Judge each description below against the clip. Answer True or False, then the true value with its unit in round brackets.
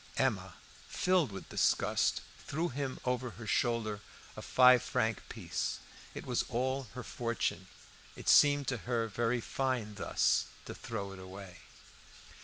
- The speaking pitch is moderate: False (120 Hz)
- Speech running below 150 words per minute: True (140 wpm)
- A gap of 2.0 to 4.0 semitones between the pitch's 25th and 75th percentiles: True (3.1 semitones)